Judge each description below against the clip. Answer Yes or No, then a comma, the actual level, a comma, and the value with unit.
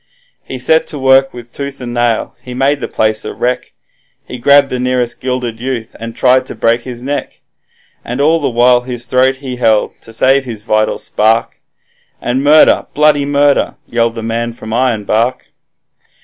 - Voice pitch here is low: Yes, low, 125 Hz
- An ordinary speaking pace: Yes, average, 175 wpm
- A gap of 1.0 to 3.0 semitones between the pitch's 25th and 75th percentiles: Yes, narrow, 2.4 semitones